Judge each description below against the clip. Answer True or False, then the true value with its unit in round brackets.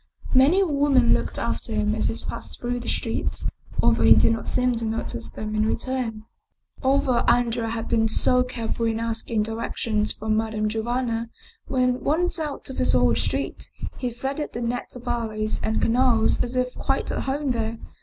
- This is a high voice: True (235 Hz)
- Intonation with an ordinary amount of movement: False (2.3 semitones)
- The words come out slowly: False (185 wpm)